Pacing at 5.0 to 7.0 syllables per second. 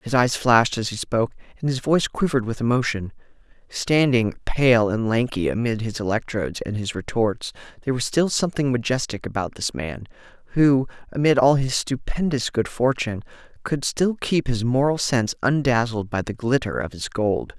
Yes: 5.3 syllables/s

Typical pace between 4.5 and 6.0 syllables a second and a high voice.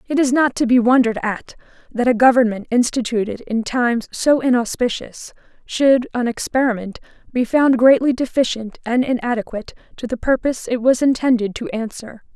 Yes: 5.4 syllables/s; high, 240 Hz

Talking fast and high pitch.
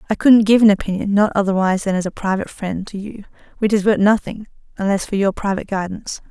Yes: fast, 210 wpm; high, 200 Hz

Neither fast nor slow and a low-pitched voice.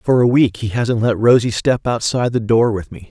No: fast, 250 wpm; low, 115 Hz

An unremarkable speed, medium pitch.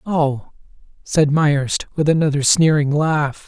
No: slow, 120 wpm; medium, 150 Hz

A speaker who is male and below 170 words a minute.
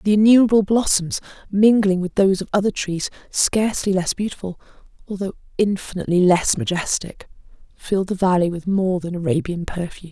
No: female; average, 140 wpm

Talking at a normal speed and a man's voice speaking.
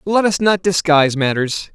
Yes: average, 170 wpm; male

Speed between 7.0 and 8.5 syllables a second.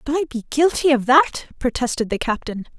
No: 5.7 syllables/s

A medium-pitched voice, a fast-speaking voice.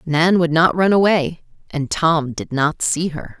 No: medium, 160 Hz; average, 195 wpm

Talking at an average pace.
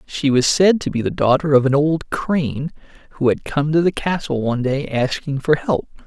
No: fast, 220 wpm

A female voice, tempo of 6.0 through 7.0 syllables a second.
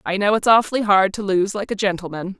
Yes: female; 6.1 syllables/s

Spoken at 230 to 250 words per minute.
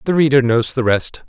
Yes: fast, 235 wpm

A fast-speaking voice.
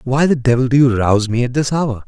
Yes: fast, 290 wpm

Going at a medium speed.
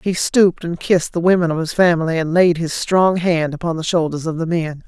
No: fast, 245 wpm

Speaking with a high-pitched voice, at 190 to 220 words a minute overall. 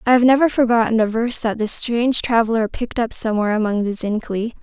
Yes: high, 225 Hz; fast, 205 wpm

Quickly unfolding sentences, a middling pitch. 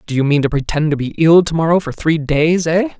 Yes: fast, 280 wpm; medium, 160 Hz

